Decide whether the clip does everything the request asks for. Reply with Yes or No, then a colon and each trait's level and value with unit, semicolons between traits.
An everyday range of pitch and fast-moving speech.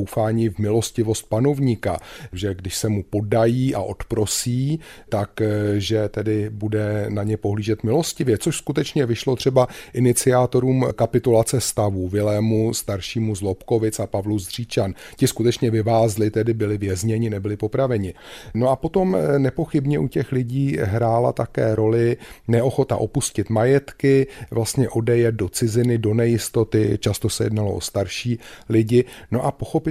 No: average, 3.1 semitones; average, 135 wpm